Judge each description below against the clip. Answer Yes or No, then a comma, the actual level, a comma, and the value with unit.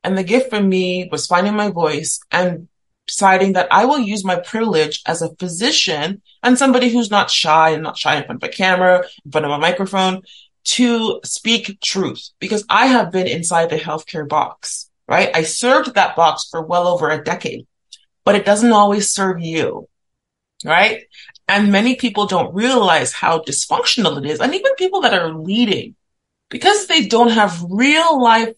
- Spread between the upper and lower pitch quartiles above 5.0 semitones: Yes, wide, 5.5 semitones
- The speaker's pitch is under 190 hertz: No, high, 195 Hz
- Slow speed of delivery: No, average, 185 wpm